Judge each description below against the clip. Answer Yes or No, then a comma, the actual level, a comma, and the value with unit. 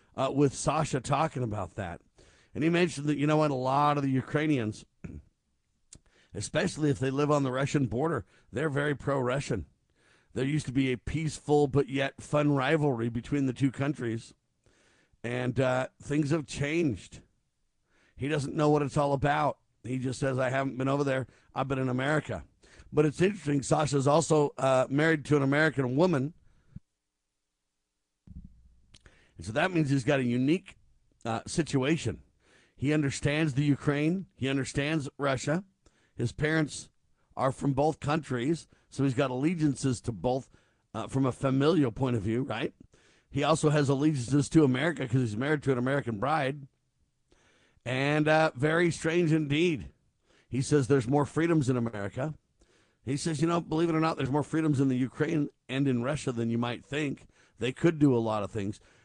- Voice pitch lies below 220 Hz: Yes, medium, 140 Hz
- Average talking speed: Yes, average, 170 wpm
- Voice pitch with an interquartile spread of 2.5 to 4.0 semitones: Yes, average, 3.4 semitones